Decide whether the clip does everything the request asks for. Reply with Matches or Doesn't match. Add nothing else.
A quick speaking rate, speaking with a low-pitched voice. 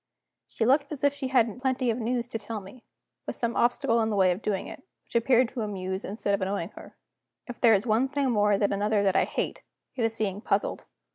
Doesn't match